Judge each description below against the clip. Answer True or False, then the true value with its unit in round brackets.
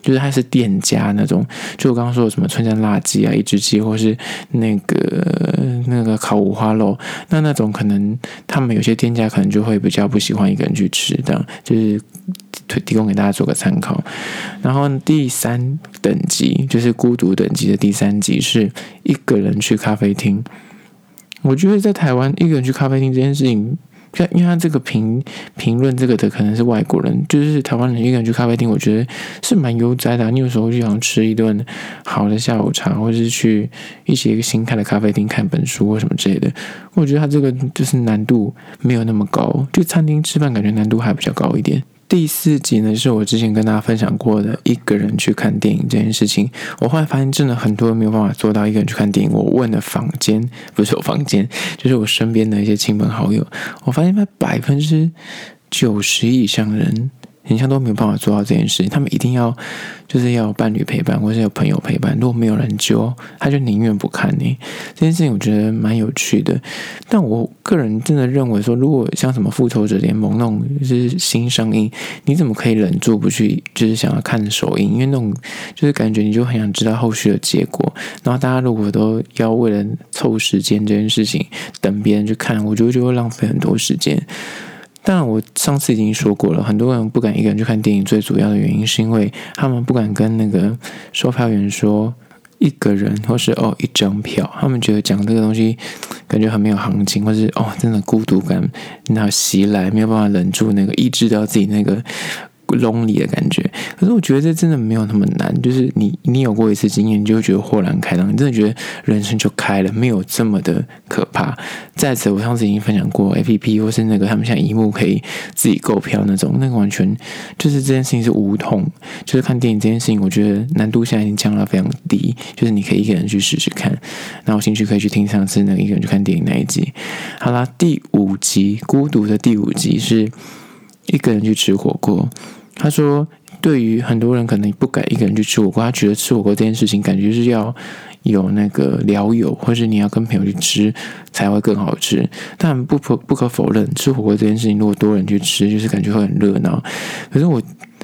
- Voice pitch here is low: True (115 Hz)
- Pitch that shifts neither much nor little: True (4.1 semitones)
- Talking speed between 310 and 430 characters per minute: True (325 characters per minute)